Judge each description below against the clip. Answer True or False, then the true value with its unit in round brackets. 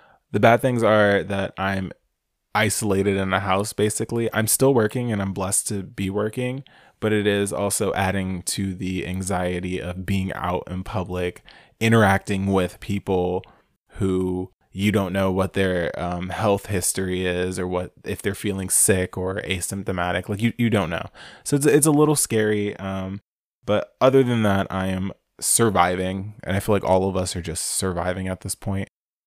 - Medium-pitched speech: False (95 Hz)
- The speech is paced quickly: False (175 wpm)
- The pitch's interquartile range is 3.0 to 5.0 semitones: False (2.4 semitones)